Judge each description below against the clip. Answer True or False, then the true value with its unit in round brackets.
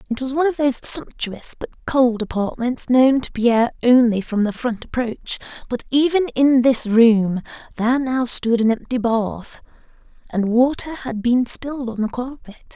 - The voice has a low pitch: False (245 Hz)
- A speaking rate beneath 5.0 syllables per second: True (4.7 syllables/s)